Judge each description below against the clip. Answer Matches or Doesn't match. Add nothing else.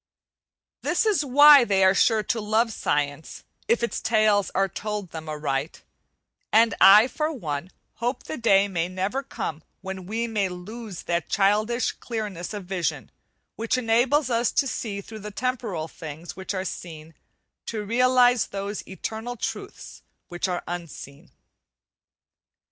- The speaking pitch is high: Matches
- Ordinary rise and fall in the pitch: Matches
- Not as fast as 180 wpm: Matches